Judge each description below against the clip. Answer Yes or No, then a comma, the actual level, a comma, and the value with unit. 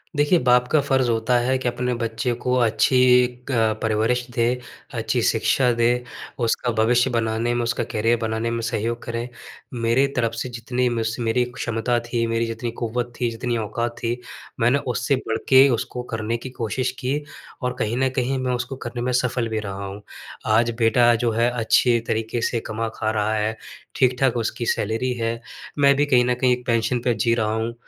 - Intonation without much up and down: Yes, narrow, 1.7 semitones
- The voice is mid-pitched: No, low, 120 Hz